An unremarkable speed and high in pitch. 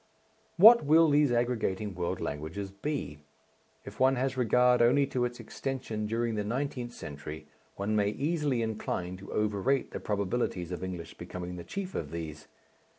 No: average, 155 wpm; low, 110 Hz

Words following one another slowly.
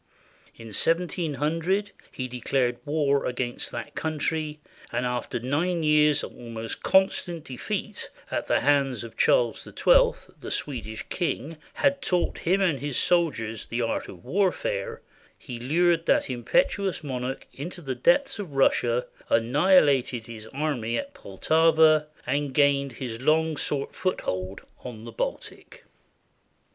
Yes: slow, 130 wpm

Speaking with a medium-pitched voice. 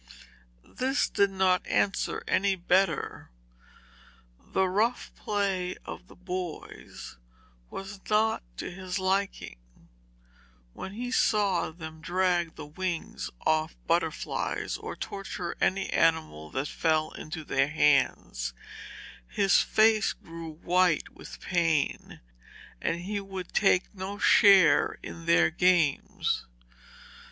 Yes: medium, 180 Hz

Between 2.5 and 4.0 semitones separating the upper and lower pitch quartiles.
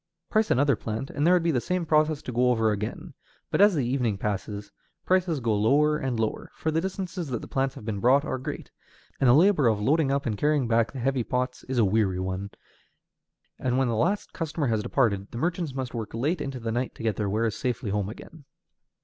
No: average, 5.3 semitones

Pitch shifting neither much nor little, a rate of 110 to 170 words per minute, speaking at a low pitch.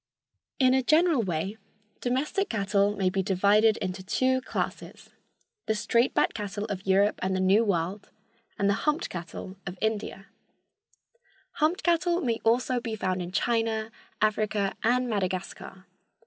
No: average, 4.2 semitones; average, 140 wpm; high, 210 Hz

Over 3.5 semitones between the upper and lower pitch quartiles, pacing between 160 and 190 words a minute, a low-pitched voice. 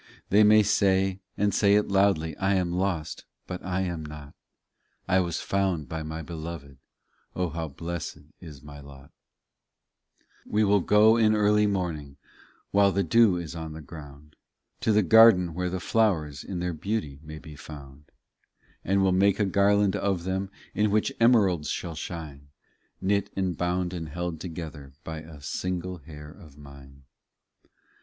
Yes: average, 4.2 semitones; average, 165 wpm; very low, 90 Hz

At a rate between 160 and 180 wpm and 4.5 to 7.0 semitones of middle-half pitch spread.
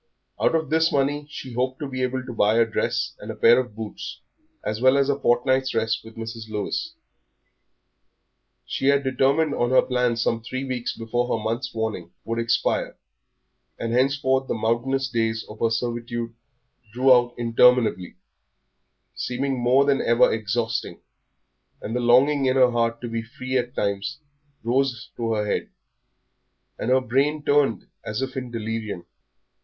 No: average, 165 wpm; narrow, 2.6 semitones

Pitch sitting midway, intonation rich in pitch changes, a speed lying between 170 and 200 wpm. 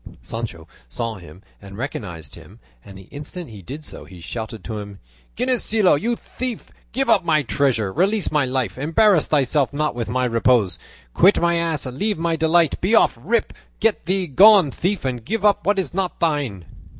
Yes: medium, 145 Hz; wide, 8.6 semitones; average, 185 wpm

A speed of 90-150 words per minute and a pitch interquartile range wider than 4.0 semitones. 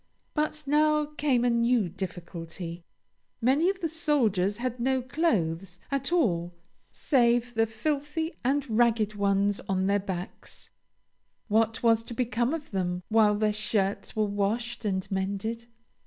Yes: average, 140 wpm; average, 5.1 semitones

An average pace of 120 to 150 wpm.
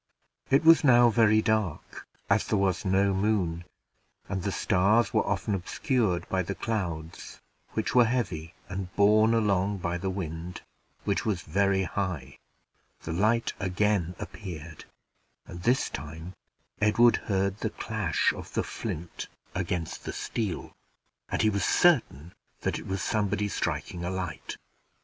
Yes: average, 145 wpm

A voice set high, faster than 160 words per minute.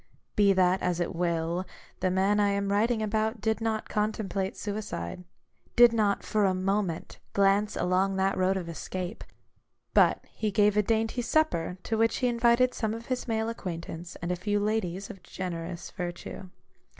Yes: high, 200 Hz; average, 170 wpm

